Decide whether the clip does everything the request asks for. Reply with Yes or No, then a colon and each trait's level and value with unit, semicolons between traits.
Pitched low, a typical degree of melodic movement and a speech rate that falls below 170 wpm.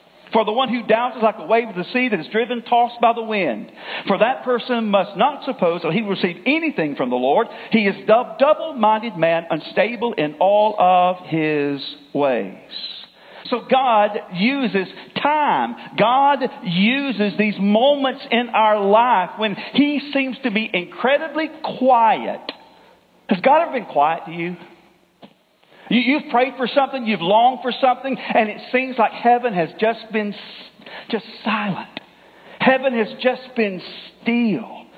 No: high, 225 Hz; average, 4.3 semitones; average, 160 wpm